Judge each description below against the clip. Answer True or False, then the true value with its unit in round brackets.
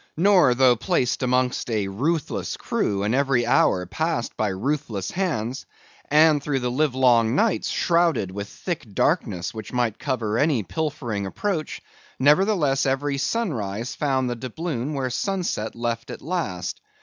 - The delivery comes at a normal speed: True (145 wpm)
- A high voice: False (130 Hz)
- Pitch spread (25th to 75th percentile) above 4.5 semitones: True (5.3 semitones)